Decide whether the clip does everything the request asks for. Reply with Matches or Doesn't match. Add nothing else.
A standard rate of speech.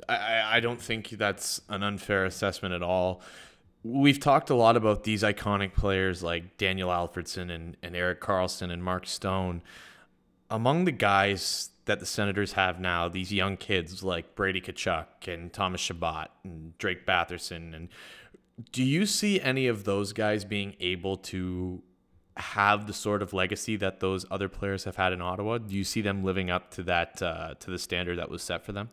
Matches